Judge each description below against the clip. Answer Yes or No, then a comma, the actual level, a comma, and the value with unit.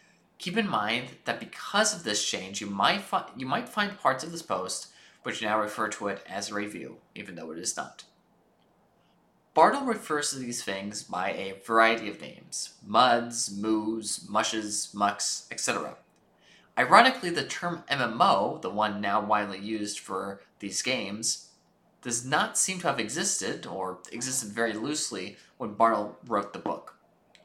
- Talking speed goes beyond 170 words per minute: No, average, 160 wpm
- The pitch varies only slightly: No, average, 4.0 semitones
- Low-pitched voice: Yes, low, 110 Hz